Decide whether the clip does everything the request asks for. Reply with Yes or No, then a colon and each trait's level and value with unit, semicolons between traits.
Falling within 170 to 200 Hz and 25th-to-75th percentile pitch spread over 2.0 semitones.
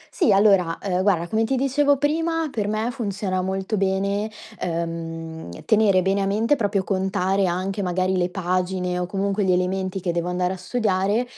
Yes: high, 190 Hz; narrow, 2.6 semitones